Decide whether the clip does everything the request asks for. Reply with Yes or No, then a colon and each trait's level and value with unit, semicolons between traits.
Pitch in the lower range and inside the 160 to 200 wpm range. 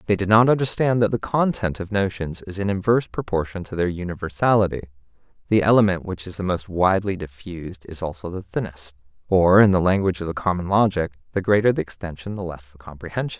Yes: very low, 95 Hz; average, 195 wpm